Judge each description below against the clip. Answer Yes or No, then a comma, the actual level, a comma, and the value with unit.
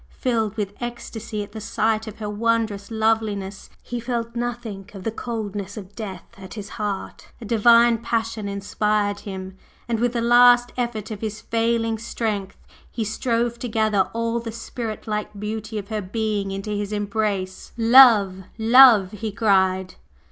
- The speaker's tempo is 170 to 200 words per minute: No, average, 160 wpm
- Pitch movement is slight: Yes, narrow, 2.2 semitones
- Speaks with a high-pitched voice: Yes, high, 220 Hz